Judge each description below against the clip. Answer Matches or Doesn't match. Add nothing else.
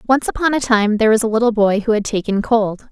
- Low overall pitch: Doesn't match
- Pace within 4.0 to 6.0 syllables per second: Doesn't match